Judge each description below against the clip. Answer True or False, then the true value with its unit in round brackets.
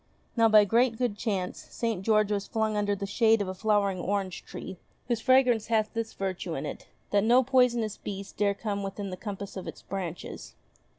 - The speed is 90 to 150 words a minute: False (195 wpm)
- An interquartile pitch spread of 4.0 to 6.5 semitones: False (2.5 semitones)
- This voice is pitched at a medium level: False (210 Hz)